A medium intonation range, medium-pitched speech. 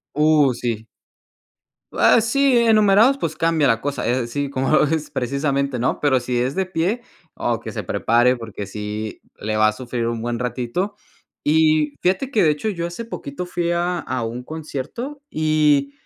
No: wide, 6.1 semitones; medium, 145 Hz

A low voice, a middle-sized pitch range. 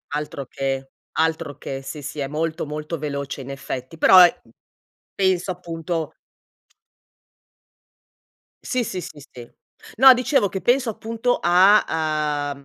No: medium, 160 Hz; average, 4.8 semitones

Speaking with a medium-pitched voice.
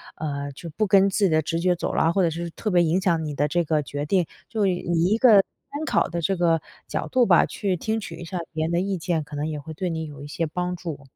Yes: medium, 170 Hz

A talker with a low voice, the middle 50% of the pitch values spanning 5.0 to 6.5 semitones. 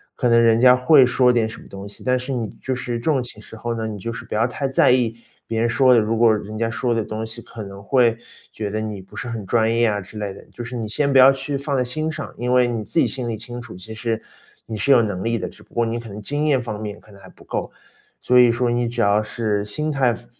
No: low, 115 Hz; narrow, 2.6 semitones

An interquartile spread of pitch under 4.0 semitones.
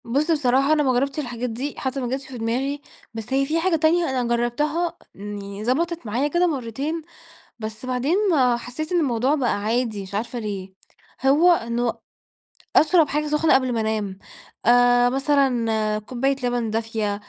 No: average, 4.4 semitones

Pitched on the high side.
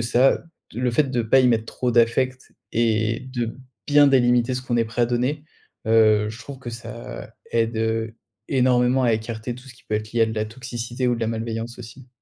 No: low, 120 Hz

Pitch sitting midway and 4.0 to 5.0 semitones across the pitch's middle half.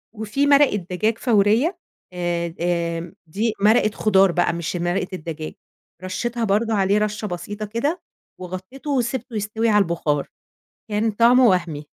No: high, 205 Hz; average, 4.5 semitones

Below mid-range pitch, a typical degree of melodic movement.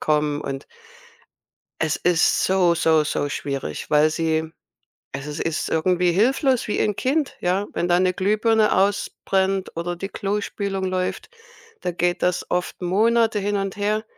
No: medium, 185 Hz; average, 4.0 semitones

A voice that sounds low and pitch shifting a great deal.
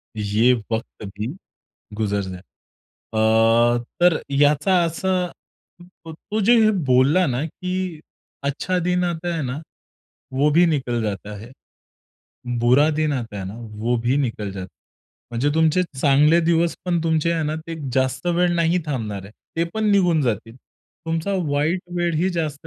No: medium, 150 Hz; wide, 5.9 semitones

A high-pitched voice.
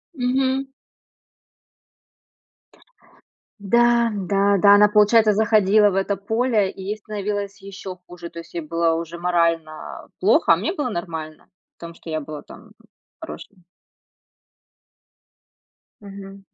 Yes: high, 200 Hz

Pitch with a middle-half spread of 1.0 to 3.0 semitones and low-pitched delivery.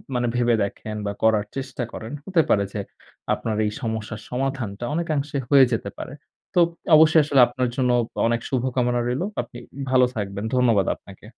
No: average, 3.4 semitones; low, 125 Hz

